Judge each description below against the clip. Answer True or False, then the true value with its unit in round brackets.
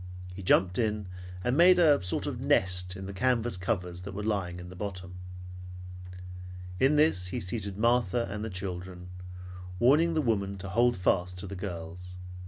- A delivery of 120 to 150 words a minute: False (175 wpm)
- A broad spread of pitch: False (4.4 semitones)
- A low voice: True (95 Hz)